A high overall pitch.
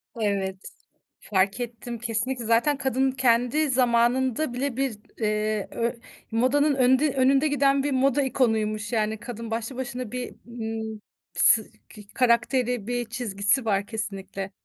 Yes: high, 240 Hz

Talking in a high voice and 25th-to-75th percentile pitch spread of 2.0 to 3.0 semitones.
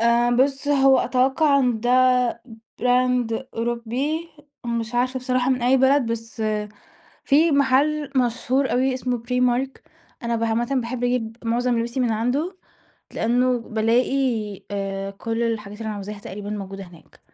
Yes: high, 245 Hz; narrow, 2.5 semitones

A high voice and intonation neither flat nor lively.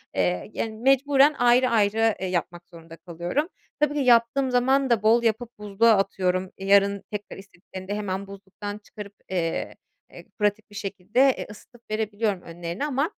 Yes: high, 210 Hz; average, 4.2 semitones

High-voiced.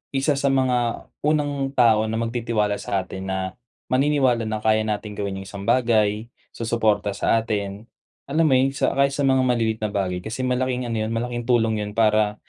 No: low, 115 Hz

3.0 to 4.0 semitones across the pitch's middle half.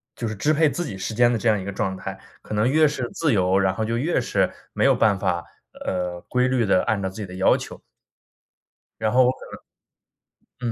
No: average, 4.8 semitones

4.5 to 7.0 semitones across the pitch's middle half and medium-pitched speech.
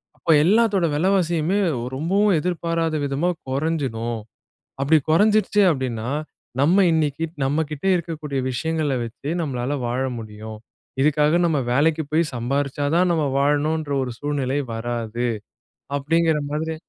No: average, 3.7 semitones; medium, 150 Hz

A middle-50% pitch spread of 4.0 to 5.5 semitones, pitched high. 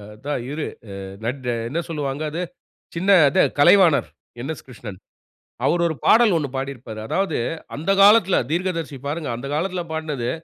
No: average, 4.6 semitones; medium, 155 Hz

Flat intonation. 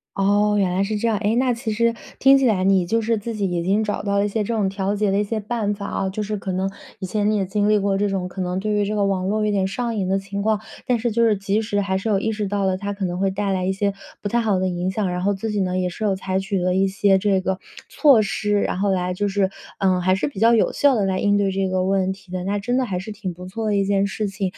Yes: narrow, 1.9 semitones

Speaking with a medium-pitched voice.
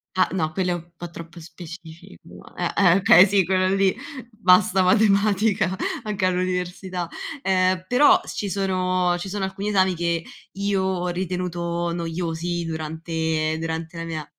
Yes: medium, 180 Hz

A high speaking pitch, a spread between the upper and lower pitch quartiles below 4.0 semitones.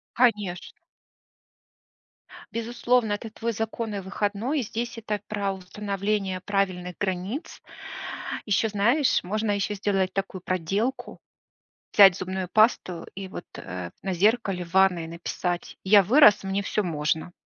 Yes: high, 200 Hz; average, 2.9 semitones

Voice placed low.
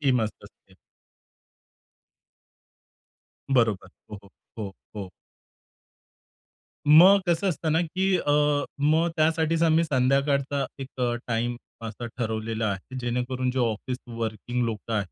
Yes: low, 130 Hz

